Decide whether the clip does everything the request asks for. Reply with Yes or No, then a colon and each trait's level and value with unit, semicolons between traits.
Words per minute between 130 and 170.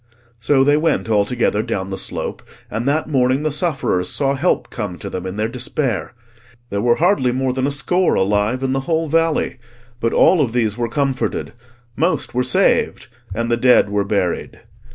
No: average, 190 wpm